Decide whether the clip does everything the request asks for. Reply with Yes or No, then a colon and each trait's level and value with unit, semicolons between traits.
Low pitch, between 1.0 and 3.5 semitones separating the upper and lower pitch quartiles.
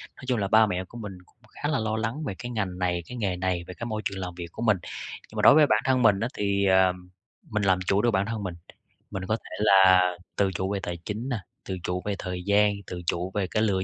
Yes: low, 100 Hz; average, 2.9 semitones